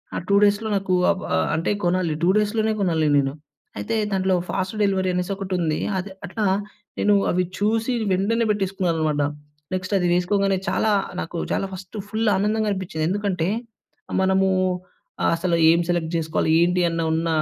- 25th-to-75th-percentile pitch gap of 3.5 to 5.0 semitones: No, average, 3.0 semitones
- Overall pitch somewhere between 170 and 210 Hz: Yes, medium, 185 Hz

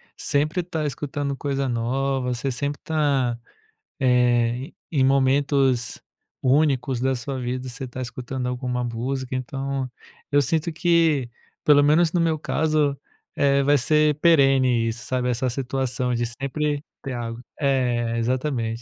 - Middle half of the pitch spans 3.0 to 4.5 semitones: No, narrow, 2.6 semitones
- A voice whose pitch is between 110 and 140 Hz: Yes, low, 135 Hz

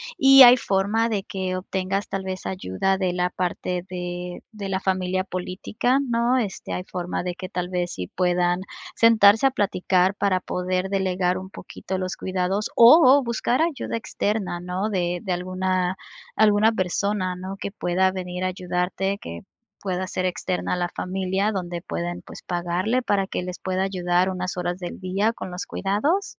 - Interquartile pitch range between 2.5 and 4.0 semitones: No, narrow, 1.9 semitones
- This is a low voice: No, medium, 185 Hz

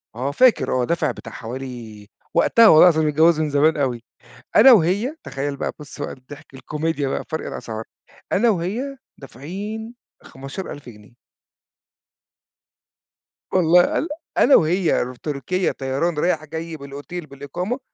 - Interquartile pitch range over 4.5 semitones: Yes, average, 5.0 semitones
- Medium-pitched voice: Yes, medium, 155 Hz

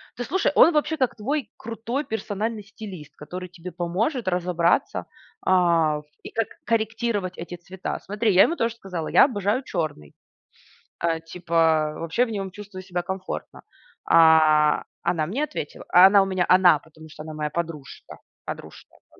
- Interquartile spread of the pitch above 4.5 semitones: Yes, average, 4.9 semitones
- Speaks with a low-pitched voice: No, medium, 185 Hz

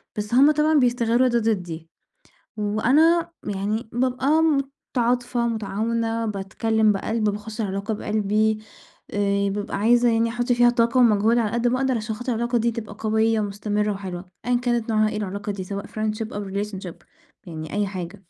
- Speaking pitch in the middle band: No, high, 220 Hz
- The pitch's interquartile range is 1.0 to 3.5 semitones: Yes, average, 2.8 semitones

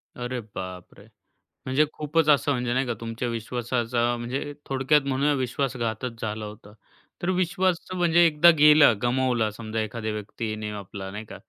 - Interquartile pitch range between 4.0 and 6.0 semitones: Yes, average, 4.7 semitones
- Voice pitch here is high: No, low, 125 Hz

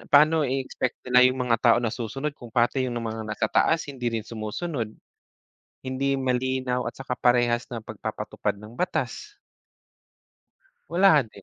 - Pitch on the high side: No, low, 125 Hz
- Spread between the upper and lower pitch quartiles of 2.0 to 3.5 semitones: Yes, average, 2.7 semitones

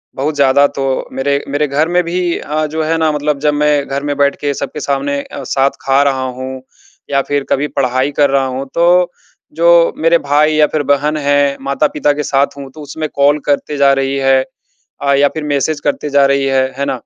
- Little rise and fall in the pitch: Yes, narrow, 1.6 semitones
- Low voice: No, medium, 145 Hz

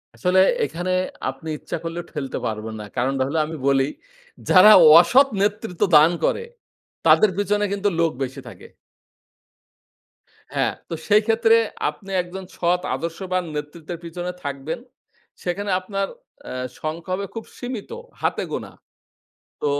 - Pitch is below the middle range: No, medium, 175 Hz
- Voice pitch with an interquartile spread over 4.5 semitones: Yes, average, 5.0 semitones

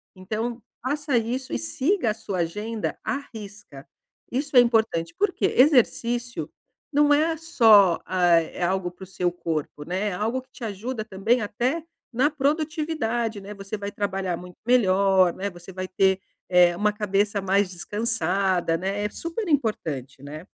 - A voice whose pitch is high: Yes, high, 205 Hz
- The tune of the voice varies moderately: Yes, average, 4.9 semitones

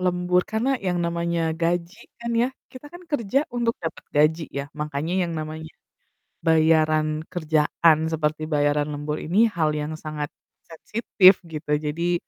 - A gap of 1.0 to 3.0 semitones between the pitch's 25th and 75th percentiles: Yes, narrow, 2.6 semitones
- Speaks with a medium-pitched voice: Yes, medium, 160 Hz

